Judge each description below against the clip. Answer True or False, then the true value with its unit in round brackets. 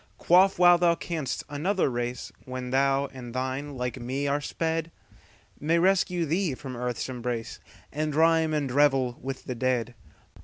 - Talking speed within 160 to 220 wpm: False (140 wpm)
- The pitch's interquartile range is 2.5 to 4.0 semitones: False (4.4 semitones)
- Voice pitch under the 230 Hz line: True (140 Hz)